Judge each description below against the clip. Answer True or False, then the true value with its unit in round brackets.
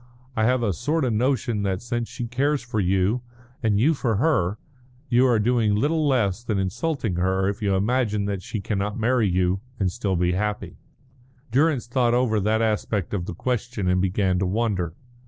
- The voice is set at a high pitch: False (110 Hz)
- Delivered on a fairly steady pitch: False (4.1 semitones)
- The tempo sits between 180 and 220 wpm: True (190 wpm)